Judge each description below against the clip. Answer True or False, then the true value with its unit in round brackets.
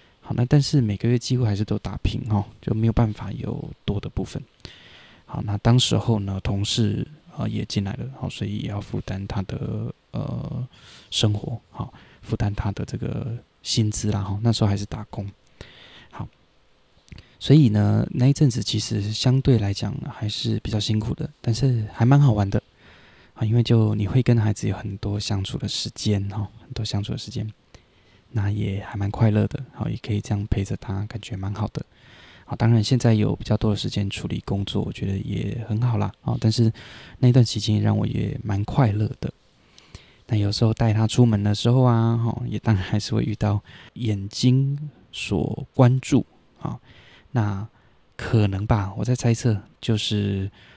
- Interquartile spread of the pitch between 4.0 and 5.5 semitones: False (2.7 semitones)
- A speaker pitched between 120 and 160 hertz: False (110 Hz)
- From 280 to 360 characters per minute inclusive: False (270 characters per minute)